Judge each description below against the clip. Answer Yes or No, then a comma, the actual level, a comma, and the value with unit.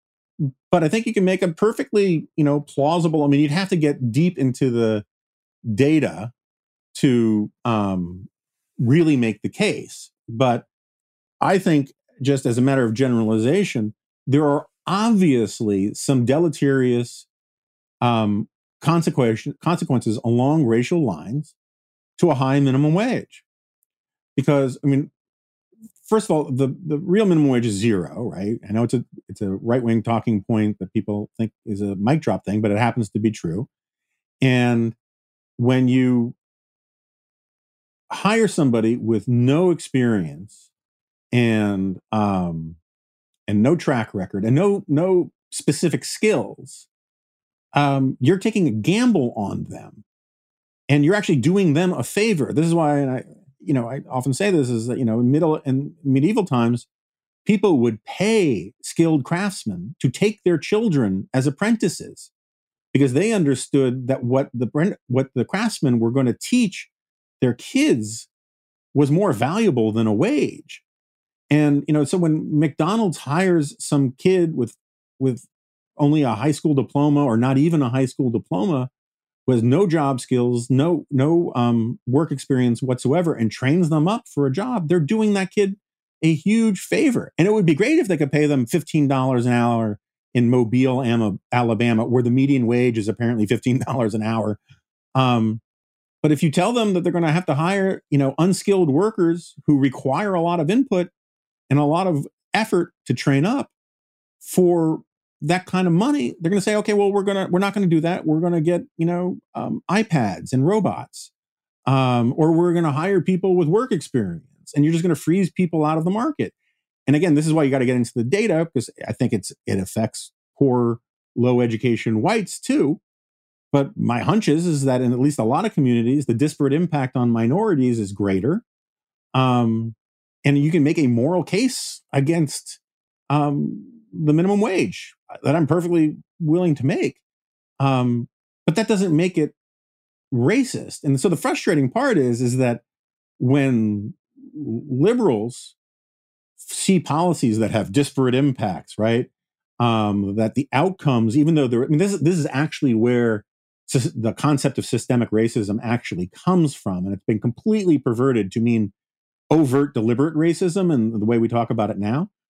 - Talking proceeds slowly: No, average, 170 wpm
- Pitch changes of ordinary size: No, wide, 6.2 semitones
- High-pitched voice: No, medium, 140 Hz